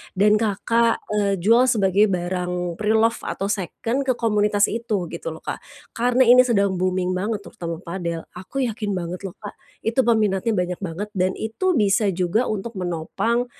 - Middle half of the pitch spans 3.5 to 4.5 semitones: Yes, average, 3.9 semitones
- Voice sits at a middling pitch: No, high, 205 Hz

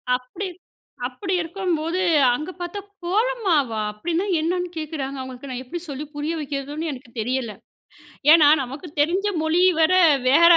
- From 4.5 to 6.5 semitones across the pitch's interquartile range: Yes, average, 4.8 semitones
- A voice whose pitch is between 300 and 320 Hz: Yes, very high, 315 Hz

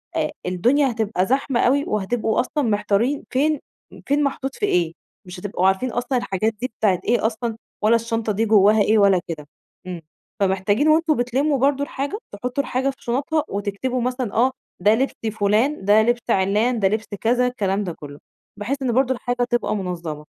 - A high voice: Yes, high, 230 Hz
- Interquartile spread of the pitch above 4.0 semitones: Yes, average, 4.5 semitones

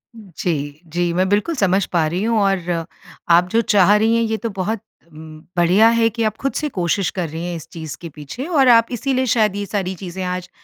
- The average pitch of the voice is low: No, high, 190 Hz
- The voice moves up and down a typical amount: Yes, average, 4.6 semitones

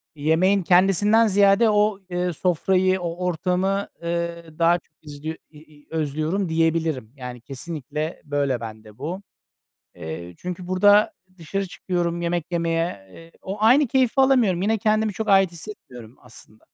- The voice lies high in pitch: No, medium, 175 Hz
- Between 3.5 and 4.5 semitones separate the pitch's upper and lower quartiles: Yes, average, 4.1 semitones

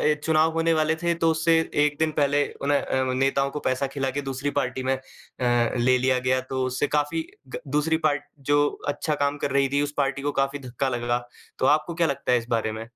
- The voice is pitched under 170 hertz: Yes, medium, 140 Hz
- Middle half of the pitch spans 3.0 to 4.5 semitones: No, narrow, 2.4 semitones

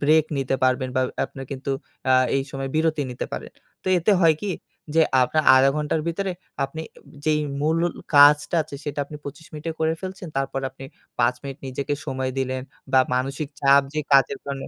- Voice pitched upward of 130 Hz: Yes, medium, 140 Hz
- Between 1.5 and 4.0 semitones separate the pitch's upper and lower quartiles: Yes, average, 2.7 semitones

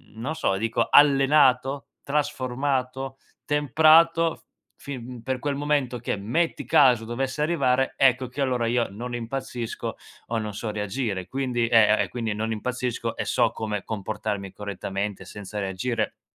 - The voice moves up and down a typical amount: Yes, average, 3.7 semitones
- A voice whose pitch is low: Yes, low, 125 Hz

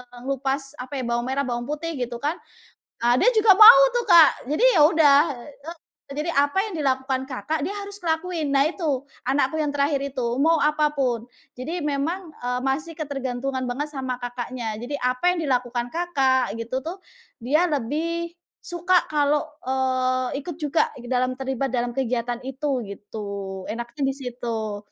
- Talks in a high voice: Yes, very high, 275 Hz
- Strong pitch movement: No, average, 3.7 semitones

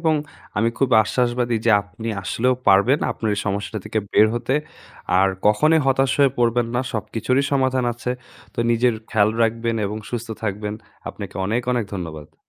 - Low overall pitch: Yes, low, 115 Hz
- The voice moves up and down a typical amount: Yes, average, 3.2 semitones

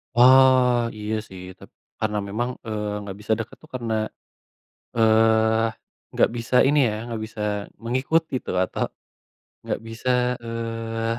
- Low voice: Yes, low, 115 Hz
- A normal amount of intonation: No, narrow, 1.8 semitones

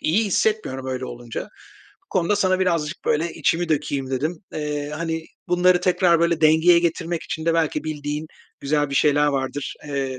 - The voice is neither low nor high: Yes, medium, 155 Hz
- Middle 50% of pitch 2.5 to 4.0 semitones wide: Yes, average, 2.9 semitones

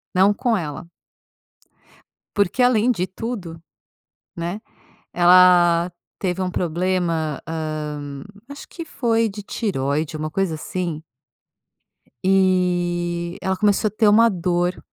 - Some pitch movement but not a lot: Yes, average, 3.3 semitones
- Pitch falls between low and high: Yes, medium, 180 Hz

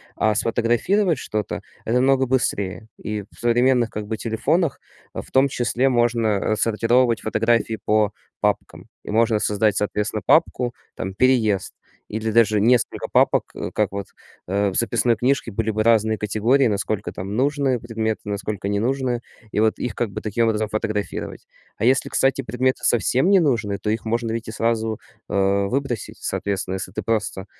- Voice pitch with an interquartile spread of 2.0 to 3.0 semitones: Yes, narrow, 2.6 semitones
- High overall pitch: No, low, 110 Hz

